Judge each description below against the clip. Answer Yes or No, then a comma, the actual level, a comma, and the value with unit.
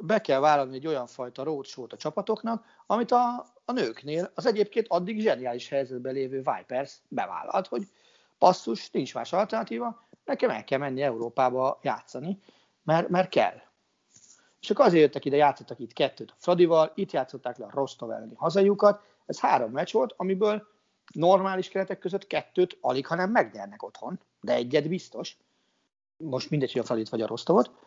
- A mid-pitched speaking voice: Yes, medium, 175 Hz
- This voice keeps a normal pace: No, fast, 165 wpm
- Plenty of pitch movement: Yes, wide, 7.2 semitones